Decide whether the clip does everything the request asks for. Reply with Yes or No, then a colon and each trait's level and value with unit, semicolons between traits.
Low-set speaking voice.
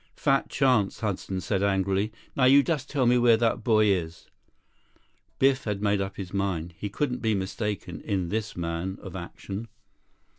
Yes: low, 100 Hz